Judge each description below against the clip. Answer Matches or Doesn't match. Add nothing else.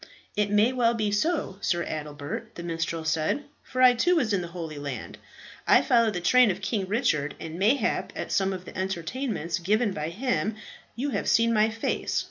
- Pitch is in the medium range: Doesn't match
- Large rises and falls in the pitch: Matches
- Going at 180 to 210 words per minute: Matches